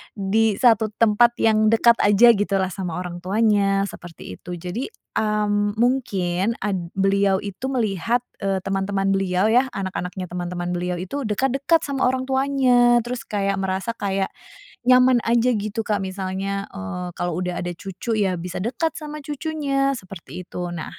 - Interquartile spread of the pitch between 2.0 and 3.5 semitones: No, average, 4.2 semitones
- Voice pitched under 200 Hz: No, high, 205 Hz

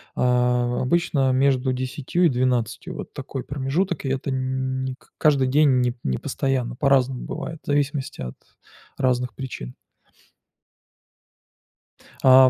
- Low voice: Yes, low, 130 Hz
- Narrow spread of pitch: Yes, narrow, 1.6 semitones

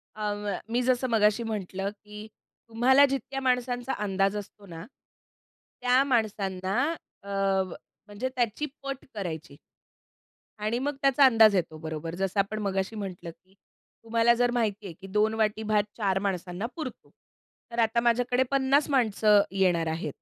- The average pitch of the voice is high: Yes, high, 210 Hz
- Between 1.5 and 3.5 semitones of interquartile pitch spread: No, average, 4.1 semitones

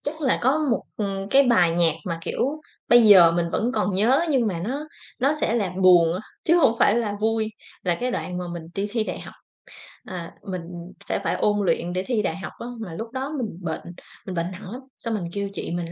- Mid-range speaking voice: No, high, 205 Hz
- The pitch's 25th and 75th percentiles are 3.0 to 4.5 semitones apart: No, average, 5.3 semitones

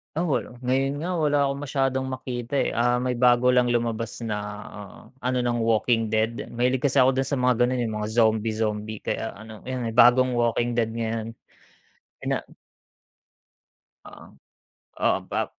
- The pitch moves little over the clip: Yes, narrow, 2.2 semitones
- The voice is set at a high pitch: No, low, 120 Hz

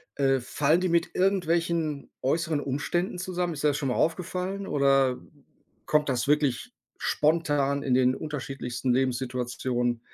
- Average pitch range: Yes, average, 4.2 semitones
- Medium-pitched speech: Yes, medium, 145 Hz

